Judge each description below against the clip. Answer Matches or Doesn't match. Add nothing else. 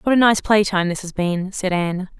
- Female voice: Matches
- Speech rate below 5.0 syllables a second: Doesn't match